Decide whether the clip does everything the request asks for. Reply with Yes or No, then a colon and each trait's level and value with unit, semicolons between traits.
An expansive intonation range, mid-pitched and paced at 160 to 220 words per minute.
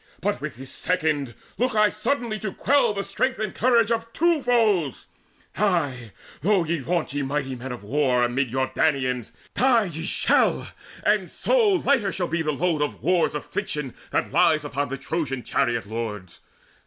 Yes: wide, 8.1 semitones; medium, 160 Hz; average, 170 wpm